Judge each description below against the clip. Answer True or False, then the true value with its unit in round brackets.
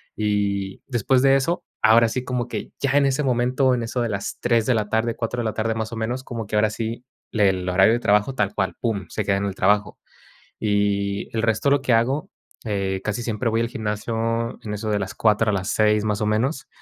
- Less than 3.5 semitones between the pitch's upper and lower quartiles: True (2.7 semitones)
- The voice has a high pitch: False (110 Hz)